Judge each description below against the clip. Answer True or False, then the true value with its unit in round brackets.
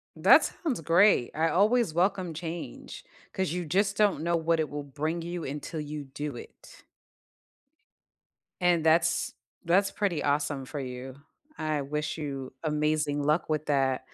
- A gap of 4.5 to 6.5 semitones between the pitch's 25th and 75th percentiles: False (3.2 semitones)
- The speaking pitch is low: False (155 Hz)